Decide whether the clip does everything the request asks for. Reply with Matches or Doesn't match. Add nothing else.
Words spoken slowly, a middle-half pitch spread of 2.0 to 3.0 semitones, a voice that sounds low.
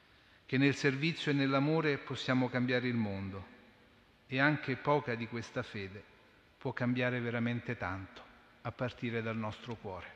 Doesn't match